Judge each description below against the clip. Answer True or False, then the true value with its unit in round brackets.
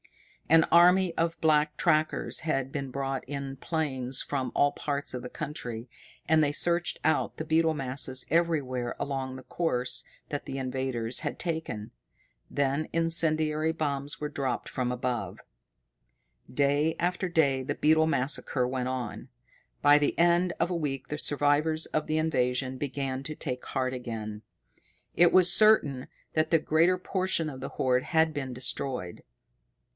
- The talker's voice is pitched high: False (145 Hz)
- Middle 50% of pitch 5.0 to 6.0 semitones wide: False (3.6 semitones)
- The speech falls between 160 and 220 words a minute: False (150 wpm)